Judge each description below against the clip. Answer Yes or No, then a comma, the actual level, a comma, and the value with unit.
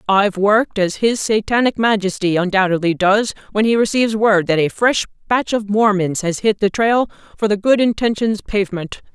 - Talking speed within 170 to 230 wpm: Yes, average, 175 wpm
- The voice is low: No, high, 205 Hz